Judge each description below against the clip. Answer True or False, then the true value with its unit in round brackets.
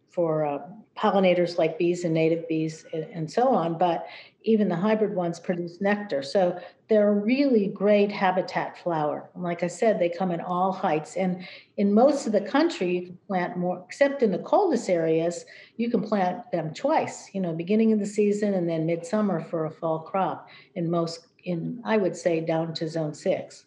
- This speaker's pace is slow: False (195 wpm)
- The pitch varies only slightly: False (3.7 semitones)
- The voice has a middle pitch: True (180 Hz)